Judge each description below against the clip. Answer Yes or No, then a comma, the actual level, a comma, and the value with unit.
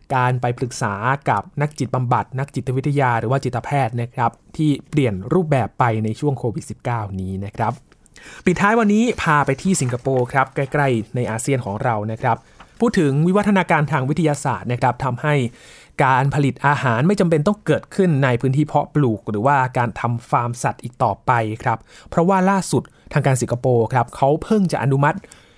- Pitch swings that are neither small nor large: Yes, average, 3.8 semitones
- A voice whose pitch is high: No, low, 135 Hz